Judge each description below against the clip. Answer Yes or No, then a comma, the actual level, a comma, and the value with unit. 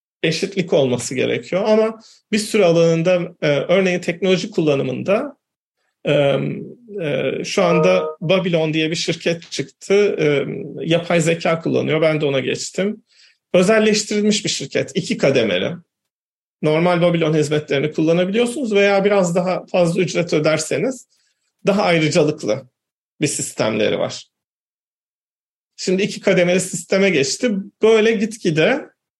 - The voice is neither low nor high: Yes, medium, 180 Hz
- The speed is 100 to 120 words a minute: Yes, average, 105 wpm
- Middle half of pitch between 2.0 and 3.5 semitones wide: No, average, 4.3 semitones